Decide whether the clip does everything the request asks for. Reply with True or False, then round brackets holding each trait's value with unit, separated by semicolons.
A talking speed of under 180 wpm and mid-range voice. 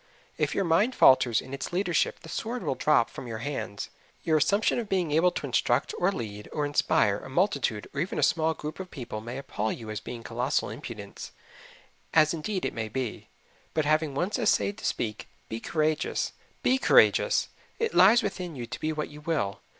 False (195 wpm; 150 Hz)